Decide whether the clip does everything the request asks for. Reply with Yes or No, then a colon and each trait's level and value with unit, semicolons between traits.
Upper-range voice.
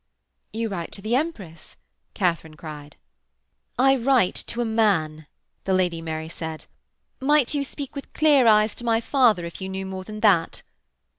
Yes: high, 205 Hz